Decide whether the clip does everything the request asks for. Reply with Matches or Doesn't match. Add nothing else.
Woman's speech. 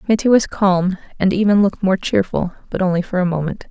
Matches